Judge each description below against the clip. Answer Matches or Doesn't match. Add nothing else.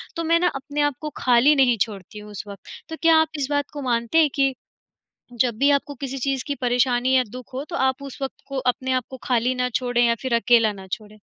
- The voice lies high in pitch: Matches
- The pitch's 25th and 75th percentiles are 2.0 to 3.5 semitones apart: Matches